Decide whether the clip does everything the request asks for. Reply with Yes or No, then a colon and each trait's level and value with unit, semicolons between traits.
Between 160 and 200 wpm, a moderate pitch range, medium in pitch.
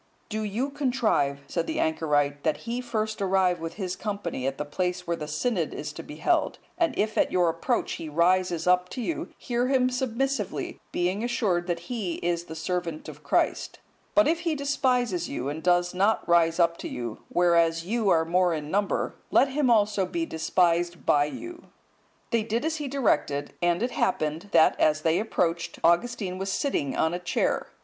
No: average, 190 wpm; wide, 6.0 semitones; medium, 180 Hz